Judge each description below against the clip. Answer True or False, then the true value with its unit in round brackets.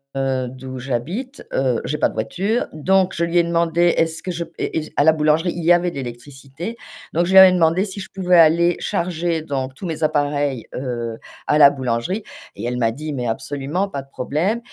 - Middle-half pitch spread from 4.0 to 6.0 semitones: True (4.7 semitones)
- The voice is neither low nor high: True (155 Hz)